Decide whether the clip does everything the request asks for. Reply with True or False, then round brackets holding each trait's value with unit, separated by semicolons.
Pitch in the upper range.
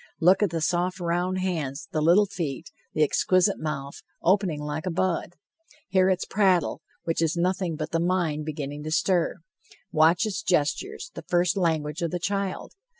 False (175 Hz)